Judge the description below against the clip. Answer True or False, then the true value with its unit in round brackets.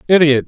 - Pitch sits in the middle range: True (150 Hz)